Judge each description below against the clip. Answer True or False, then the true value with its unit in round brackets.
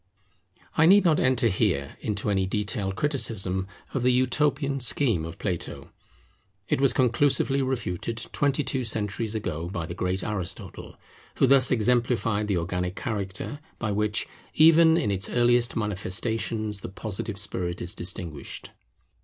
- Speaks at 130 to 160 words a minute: True (140 wpm)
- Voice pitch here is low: True (110 Hz)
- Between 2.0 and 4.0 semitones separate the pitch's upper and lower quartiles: False (5.2 semitones)